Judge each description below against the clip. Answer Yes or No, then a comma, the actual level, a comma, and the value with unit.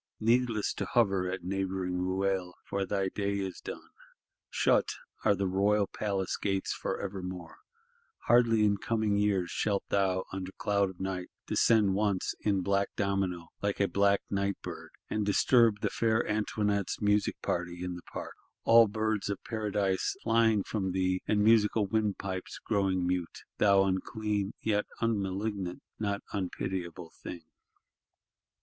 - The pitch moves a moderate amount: No, narrow, 1.9 semitones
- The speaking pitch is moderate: No, low, 100 Hz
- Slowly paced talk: No, average, 145 wpm